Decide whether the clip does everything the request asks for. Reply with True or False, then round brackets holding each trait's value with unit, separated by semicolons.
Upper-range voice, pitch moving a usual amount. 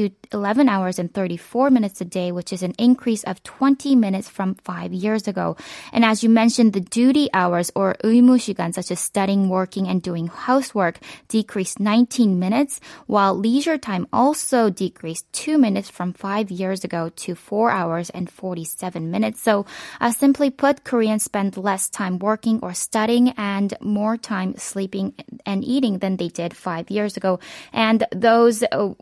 True (205 Hz; 3.8 semitones)